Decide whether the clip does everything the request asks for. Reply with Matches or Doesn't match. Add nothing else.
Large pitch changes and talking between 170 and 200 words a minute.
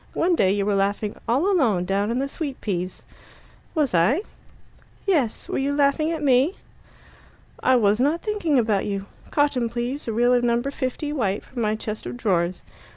Matches